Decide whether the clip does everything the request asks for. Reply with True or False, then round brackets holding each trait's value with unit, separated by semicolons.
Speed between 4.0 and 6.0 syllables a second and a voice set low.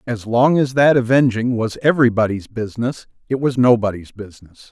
True (5.5 syllables/s; 120 Hz)